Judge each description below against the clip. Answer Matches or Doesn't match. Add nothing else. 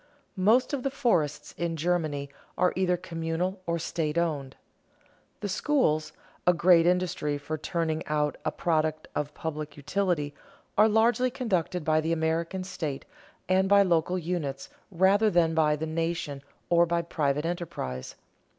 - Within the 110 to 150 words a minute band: Matches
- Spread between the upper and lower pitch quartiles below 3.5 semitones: Matches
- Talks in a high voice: Doesn't match